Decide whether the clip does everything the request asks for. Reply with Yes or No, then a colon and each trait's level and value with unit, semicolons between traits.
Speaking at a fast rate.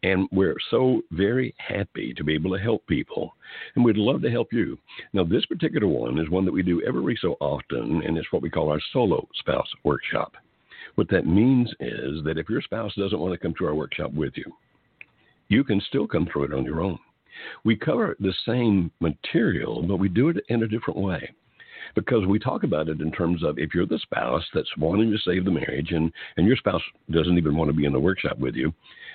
Yes: fast, 225 wpm